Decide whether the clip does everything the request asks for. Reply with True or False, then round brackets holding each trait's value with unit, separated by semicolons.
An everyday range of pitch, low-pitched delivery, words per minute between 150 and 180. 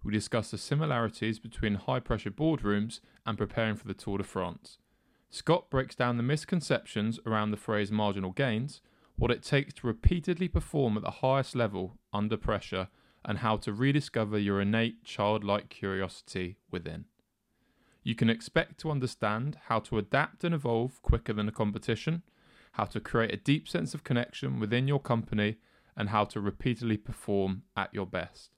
True (4.1 semitones; 110 Hz; 165 wpm)